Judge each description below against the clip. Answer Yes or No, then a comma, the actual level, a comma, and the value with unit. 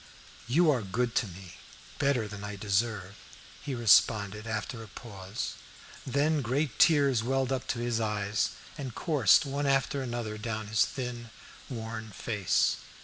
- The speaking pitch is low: Yes, low, 115 Hz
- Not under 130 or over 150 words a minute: Yes, average, 145 wpm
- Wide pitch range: No, average, 4.0 semitones